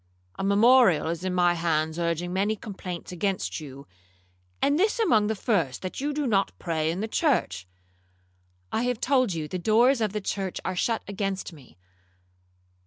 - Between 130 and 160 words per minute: No, average, 170 wpm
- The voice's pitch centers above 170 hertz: Yes, medium, 185 Hz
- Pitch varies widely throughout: Yes, wide, 5.7 semitones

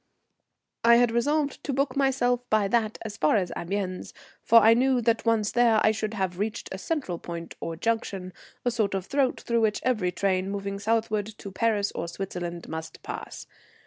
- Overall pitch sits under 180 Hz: No, high, 215 Hz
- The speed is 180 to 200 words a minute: Yes, average, 185 wpm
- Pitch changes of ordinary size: Yes, average, 3.7 semitones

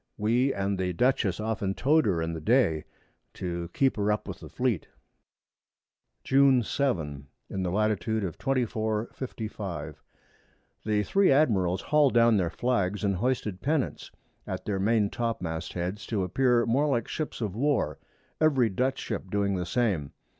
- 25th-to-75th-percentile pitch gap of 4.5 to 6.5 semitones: Yes, average, 5.2 semitones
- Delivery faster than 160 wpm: No, average, 155 wpm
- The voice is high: No, low, 105 Hz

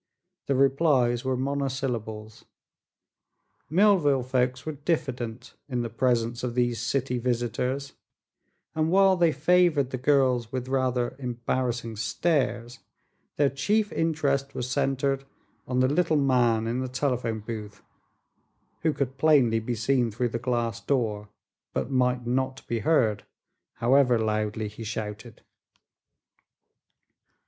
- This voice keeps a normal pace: No, slow, 120 wpm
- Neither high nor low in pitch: No, low, 125 Hz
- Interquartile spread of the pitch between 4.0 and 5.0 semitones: No, average, 2.8 semitones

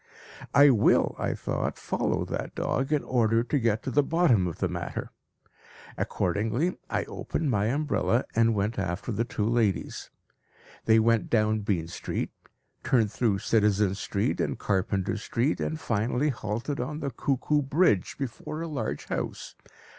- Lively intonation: No, average, 4.8 semitones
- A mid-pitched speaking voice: No, low, 115 Hz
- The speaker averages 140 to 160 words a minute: Yes, average, 155 wpm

